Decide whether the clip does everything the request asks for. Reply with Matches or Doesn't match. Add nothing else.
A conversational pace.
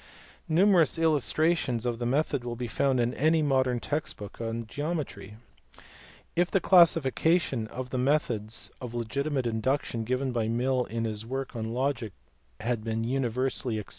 Matches